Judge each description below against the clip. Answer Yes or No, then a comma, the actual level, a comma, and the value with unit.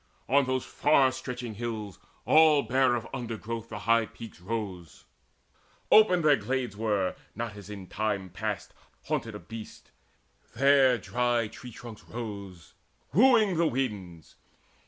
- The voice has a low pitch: Yes, low, 115 Hz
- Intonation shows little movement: No, average, 3.9 semitones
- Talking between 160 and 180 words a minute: No, slow, 135 wpm